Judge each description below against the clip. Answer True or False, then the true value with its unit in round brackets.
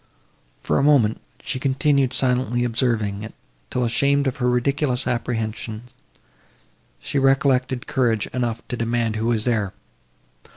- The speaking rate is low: True (130 wpm)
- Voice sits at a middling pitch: False (125 Hz)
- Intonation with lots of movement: False (2.6 semitones)